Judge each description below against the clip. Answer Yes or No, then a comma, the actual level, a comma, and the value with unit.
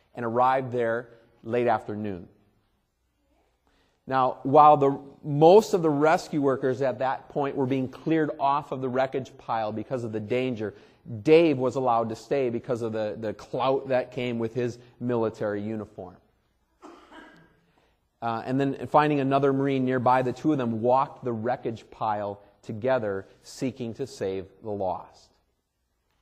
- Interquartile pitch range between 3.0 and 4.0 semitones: Yes, average, 3.4 semitones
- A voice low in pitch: Yes, low, 125 Hz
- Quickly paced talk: No, average, 150 wpm